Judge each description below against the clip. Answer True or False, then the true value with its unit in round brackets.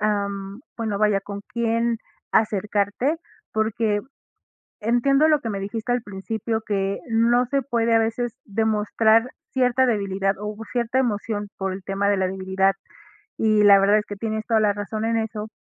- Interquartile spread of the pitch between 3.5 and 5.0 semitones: False (2.4 semitones)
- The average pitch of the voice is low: False (215 Hz)